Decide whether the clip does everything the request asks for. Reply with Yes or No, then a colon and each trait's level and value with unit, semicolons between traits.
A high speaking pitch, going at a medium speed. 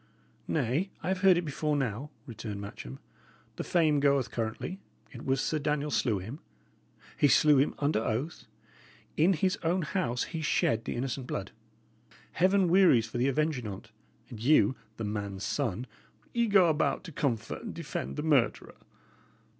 No: medium, 140 Hz; average, 160 wpm